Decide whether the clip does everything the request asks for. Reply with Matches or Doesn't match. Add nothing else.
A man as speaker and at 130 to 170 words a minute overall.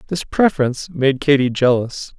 Matches